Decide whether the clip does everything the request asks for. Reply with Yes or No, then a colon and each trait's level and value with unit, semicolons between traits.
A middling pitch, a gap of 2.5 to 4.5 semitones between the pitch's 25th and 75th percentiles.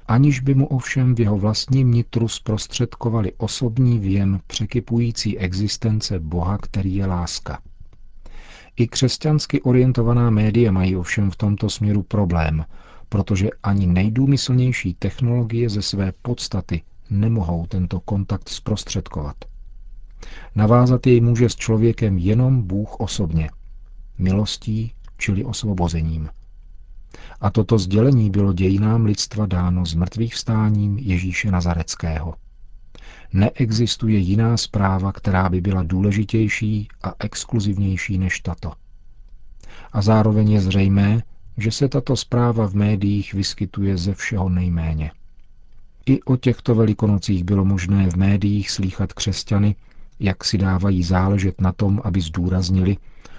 No: low, 100 Hz; average, 3.3 semitones